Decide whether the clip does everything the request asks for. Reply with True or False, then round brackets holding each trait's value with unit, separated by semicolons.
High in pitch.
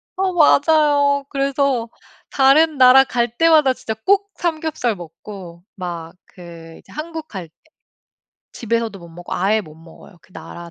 True (240 Hz)